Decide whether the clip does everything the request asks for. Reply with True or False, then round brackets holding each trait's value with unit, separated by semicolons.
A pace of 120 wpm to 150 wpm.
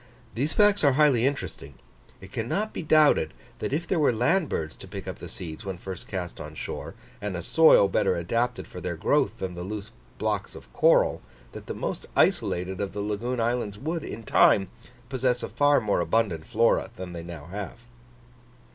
False (190 wpm)